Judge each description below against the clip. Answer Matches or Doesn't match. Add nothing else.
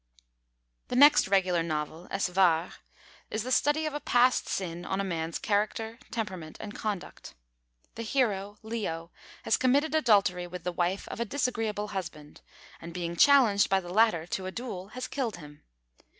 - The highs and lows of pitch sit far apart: Doesn't match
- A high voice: Matches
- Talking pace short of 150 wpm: Doesn't match